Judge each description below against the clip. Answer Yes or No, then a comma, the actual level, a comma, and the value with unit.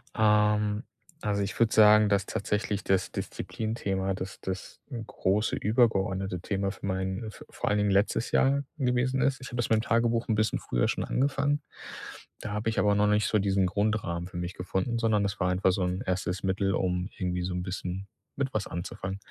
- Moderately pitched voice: No, low, 100 Hz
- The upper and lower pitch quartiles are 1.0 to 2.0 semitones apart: No, narrow, 2.6 semitones